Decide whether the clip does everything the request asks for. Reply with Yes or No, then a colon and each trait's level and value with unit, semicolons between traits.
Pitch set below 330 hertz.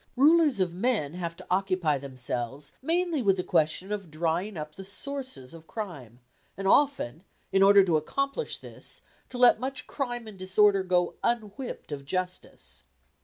Yes: high, 190 Hz